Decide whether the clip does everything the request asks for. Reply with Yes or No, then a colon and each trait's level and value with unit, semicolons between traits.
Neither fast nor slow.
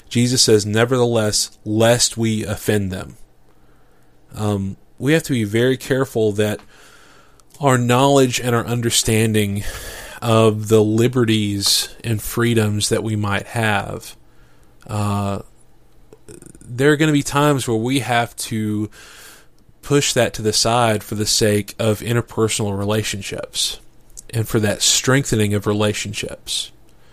No: slow, 125 wpm